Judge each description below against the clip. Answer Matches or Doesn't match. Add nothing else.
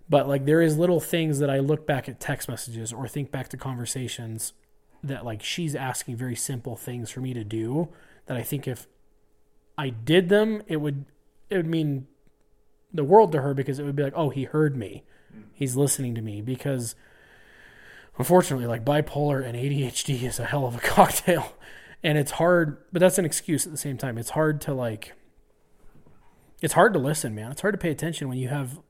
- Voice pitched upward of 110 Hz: Matches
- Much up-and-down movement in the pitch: Doesn't match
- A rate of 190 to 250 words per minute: Matches